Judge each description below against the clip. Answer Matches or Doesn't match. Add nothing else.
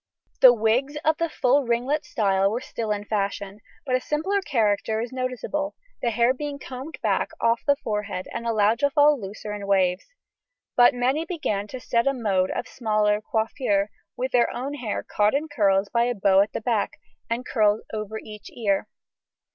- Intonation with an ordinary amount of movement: Matches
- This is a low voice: Doesn't match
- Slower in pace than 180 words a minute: Doesn't match